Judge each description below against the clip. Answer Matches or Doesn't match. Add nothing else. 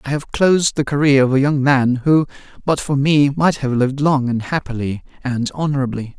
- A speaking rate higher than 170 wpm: Matches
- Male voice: Matches